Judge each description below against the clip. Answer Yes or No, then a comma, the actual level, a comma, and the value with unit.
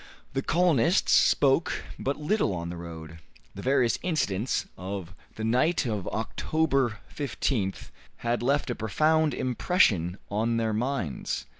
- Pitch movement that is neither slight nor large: No, wide, 6.4 semitones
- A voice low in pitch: Yes, low, 120 Hz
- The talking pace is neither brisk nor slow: No, slow, 130 wpm